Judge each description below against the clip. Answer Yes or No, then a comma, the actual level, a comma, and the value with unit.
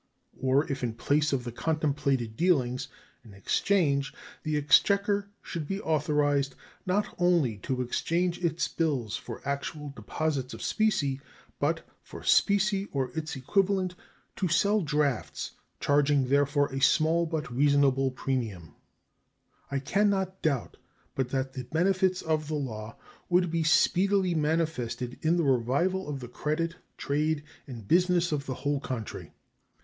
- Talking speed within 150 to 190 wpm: No, average, 140 wpm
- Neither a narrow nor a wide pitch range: Yes, average, 4.5 semitones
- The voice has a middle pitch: Yes, medium, 150 Hz